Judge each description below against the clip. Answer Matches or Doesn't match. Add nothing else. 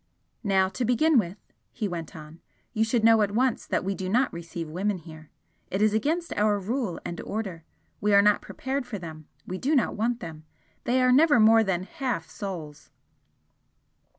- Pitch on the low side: Doesn't match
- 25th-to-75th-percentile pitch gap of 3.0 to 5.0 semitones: Doesn't match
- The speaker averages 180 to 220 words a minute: Matches